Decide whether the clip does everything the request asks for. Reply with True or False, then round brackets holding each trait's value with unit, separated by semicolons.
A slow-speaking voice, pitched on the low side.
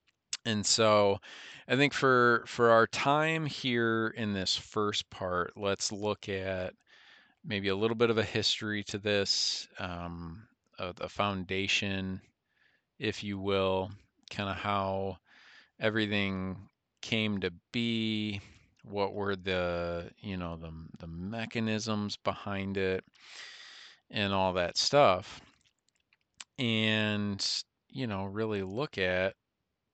True (120 wpm; 100 Hz)